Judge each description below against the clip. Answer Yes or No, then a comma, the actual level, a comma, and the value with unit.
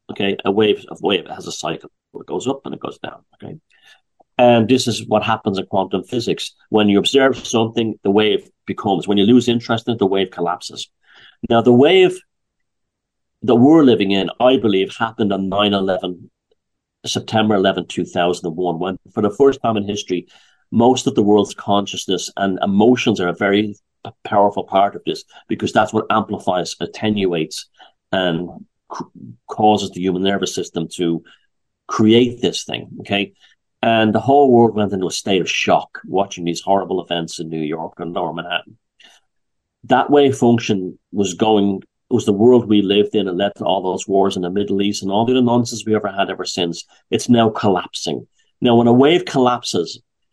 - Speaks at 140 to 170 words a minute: No, average, 180 wpm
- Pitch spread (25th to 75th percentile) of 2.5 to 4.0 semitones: Yes, average, 3.5 semitones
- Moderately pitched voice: No, low, 105 Hz